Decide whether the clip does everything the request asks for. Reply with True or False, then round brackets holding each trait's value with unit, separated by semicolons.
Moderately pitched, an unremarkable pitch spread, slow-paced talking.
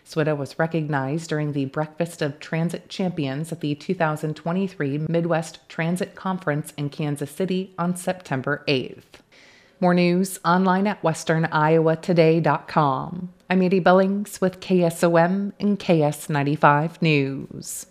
True (165 Hz; 3.6 semitones; 115 wpm)